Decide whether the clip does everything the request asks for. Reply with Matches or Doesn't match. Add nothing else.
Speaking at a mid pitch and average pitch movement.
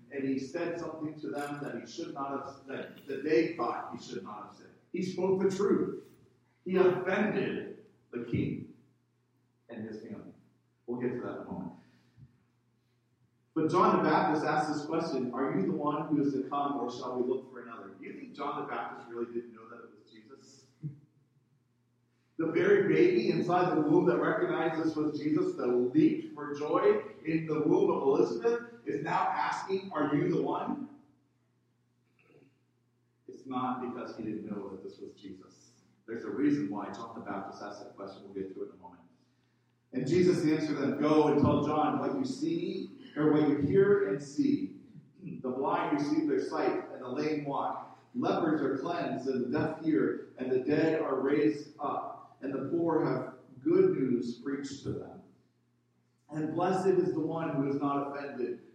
Doesn't match